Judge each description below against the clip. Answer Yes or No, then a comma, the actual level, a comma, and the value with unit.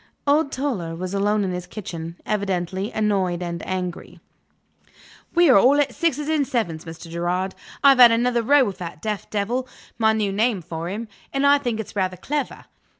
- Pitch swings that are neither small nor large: No, wide, 5.9 semitones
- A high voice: Yes, high, 205 Hz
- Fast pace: No, average, 180 wpm